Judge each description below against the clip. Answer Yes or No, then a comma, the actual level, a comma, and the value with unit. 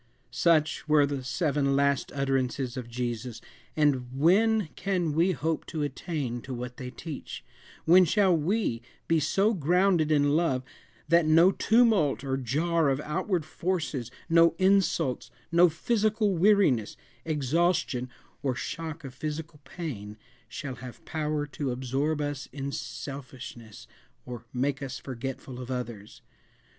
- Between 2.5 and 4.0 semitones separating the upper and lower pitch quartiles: No, average, 4.6 semitones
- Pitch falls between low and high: Yes, medium, 145 Hz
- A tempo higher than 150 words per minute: No, slow, 135 wpm